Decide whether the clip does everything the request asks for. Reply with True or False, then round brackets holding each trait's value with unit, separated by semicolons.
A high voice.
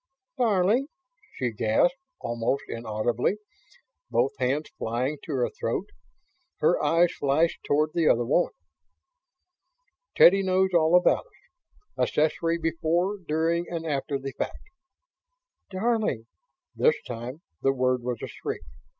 False (155 Hz)